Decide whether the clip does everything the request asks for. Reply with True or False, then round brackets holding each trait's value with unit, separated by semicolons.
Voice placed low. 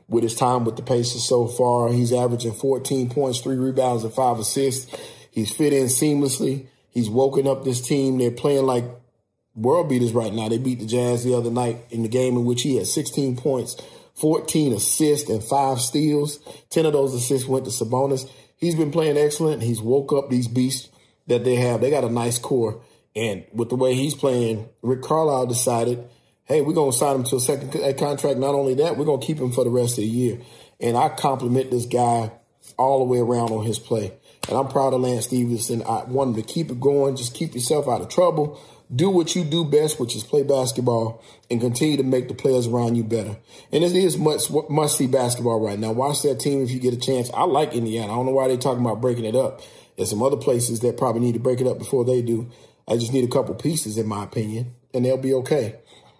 True (125 Hz)